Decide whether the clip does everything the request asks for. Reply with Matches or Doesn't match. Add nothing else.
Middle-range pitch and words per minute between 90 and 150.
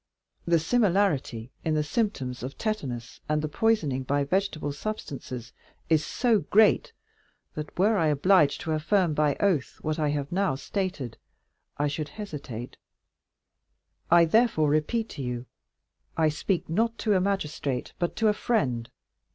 Matches